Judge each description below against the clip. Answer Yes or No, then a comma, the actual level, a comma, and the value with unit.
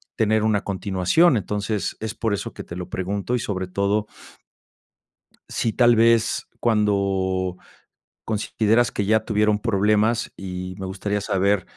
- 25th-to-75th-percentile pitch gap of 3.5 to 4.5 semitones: No, narrow, 2.4 semitones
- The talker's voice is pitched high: No, low, 105 Hz